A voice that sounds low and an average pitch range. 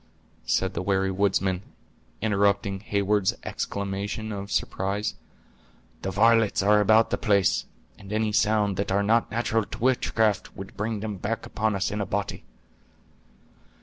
No: low, 100 Hz; narrow, 1.8 semitones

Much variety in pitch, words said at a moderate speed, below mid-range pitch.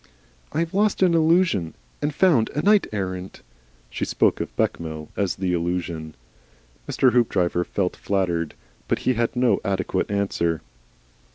Yes: wide, 8.6 semitones; average, 145 wpm; low, 100 Hz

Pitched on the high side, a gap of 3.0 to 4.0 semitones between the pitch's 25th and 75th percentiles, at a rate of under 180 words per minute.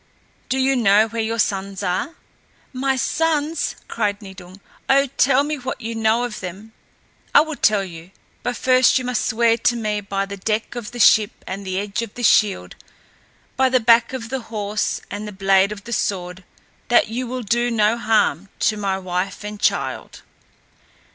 No: high, 220 Hz; average, 3.6 semitones; average, 185 wpm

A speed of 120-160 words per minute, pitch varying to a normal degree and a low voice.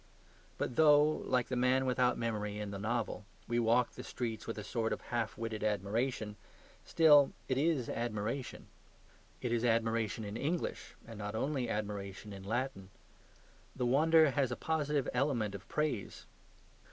Yes: average, 155 wpm; average, 3.9 semitones; low, 120 Hz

